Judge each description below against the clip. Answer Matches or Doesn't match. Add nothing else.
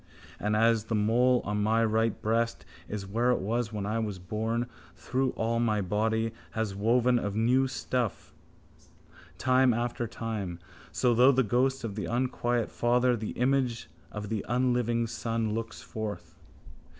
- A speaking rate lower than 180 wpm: Matches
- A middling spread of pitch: Doesn't match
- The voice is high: Doesn't match